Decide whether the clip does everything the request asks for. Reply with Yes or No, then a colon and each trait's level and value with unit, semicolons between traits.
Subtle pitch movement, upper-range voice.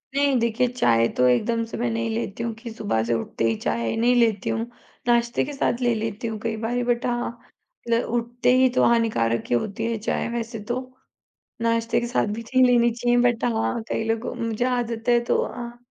Yes: narrow, 1.5 semitones; high, 230 Hz